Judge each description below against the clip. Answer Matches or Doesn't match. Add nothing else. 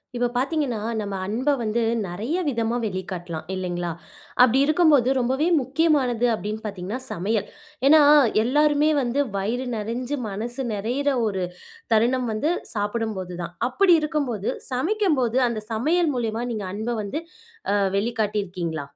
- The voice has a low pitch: Doesn't match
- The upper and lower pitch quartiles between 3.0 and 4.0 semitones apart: Doesn't match